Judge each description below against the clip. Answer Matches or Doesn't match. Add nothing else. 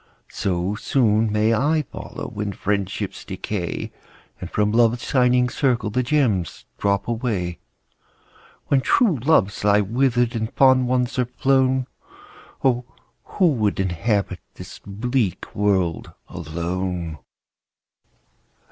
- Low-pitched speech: Matches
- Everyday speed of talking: Doesn't match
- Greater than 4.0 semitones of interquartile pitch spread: Matches